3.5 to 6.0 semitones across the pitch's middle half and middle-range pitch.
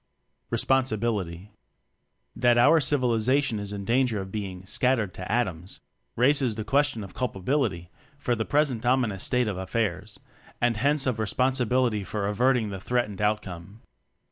No: average, 4.2 semitones; low, 115 Hz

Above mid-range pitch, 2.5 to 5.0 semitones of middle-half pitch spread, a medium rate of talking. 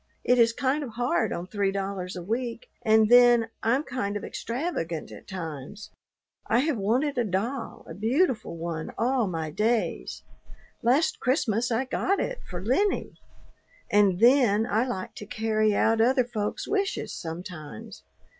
Yes: high, 225 Hz; average, 4.4 semitones; average, 155 wpm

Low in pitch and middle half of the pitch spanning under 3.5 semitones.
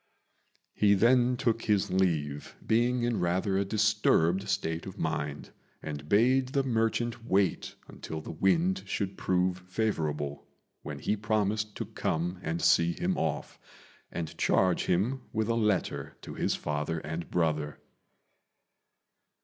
No: very low, 95 Hz; wide, 5.5 semitones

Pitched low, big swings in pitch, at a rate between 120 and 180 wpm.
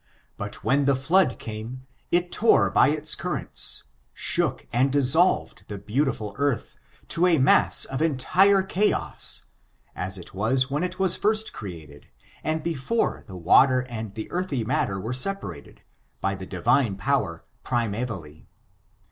Yes: low, 130 Hz; wide, 7.3 semitones; average, 145 wpm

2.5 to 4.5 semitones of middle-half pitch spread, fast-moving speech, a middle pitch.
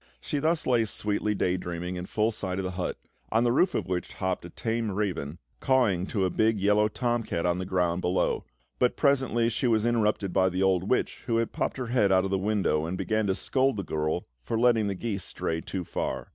No: average, 4.1 semitones; fast, 230 wpm; low, 100 Hz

